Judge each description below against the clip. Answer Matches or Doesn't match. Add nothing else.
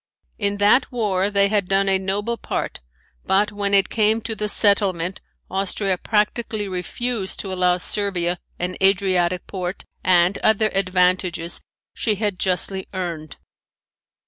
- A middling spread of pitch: Doesn't match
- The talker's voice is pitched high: Matches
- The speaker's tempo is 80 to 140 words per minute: Matches